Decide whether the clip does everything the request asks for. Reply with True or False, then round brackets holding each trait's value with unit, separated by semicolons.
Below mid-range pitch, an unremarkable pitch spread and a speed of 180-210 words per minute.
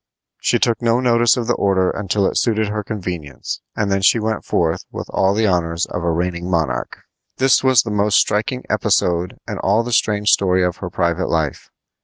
True (100 Hz; 4.0 semitones; 200 wpm)